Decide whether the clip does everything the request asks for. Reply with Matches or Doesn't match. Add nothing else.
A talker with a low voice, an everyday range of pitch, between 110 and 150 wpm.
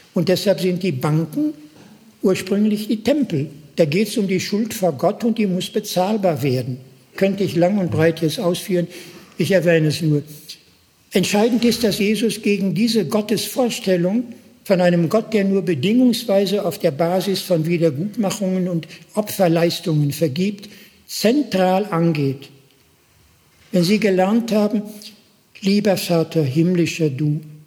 Doesn't match